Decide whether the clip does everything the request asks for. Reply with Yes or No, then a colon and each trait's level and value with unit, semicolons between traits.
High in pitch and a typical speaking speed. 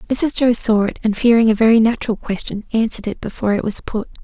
No: high, 220 Hz; fast, 225 wpm